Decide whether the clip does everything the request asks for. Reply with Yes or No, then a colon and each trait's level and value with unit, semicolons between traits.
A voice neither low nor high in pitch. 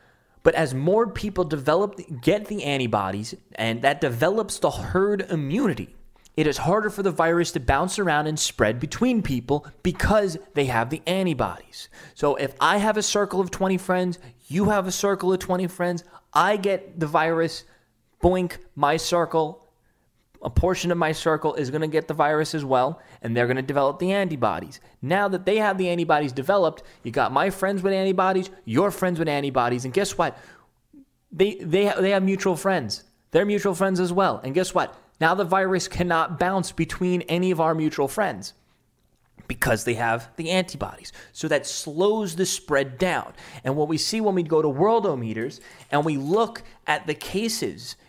Yes: medium, 170 Hz